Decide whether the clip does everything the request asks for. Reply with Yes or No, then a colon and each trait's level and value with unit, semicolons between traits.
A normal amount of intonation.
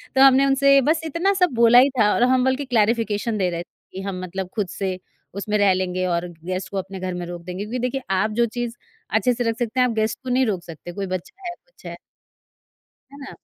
No: wide, 5.7 semitones